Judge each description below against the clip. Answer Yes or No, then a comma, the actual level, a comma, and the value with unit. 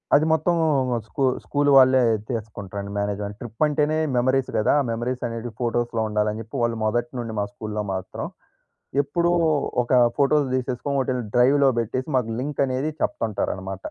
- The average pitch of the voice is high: No, low, 120 Hz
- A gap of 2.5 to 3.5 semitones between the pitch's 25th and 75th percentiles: No, average, 4.1 semitones